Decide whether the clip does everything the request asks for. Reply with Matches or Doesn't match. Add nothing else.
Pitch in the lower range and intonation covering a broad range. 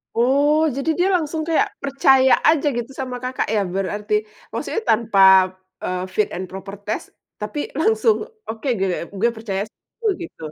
Doesn't match